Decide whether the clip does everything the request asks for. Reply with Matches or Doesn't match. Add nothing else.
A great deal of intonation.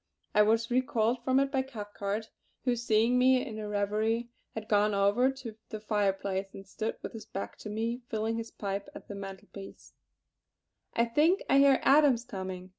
Doesn't match